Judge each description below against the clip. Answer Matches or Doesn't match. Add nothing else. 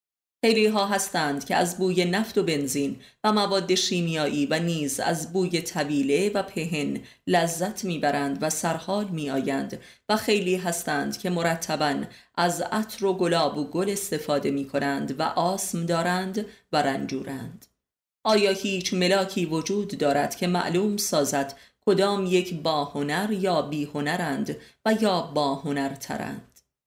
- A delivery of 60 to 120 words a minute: Doesn't match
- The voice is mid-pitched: Matches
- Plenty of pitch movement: Doesn't match